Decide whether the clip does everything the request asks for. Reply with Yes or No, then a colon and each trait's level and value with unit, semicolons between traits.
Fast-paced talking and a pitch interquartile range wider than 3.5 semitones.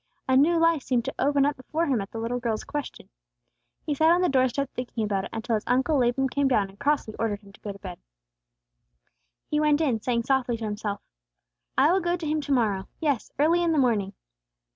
Yes: fast, 225 wpm; average, 5.0 semitones